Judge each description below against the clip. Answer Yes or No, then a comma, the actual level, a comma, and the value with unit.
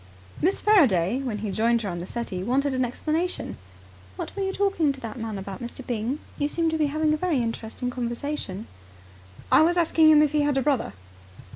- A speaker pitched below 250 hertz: No, very high, 270 Hz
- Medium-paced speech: No, fast, 210 wpm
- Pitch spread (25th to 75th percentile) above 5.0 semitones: Yes, wide, 5.4 semitones